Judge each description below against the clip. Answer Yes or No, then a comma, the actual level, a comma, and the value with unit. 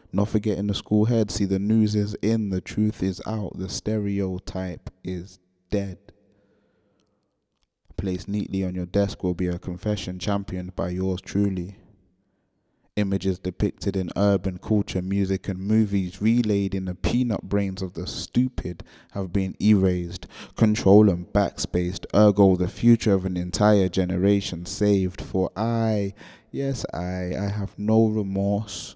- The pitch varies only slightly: Yes, narrow, 2.0 semitones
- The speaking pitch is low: Yes, low, 100 Hz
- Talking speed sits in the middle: Yes, average, 145 wpm